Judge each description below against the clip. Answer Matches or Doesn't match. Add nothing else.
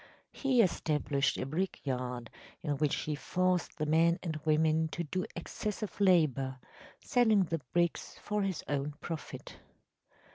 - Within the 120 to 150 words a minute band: Matches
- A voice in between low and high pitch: Matches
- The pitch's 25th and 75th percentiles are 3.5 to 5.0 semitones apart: Matches